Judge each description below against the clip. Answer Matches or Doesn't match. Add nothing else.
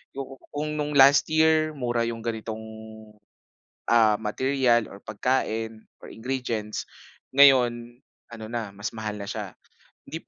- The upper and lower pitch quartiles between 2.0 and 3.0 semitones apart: Doesn't match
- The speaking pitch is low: Matches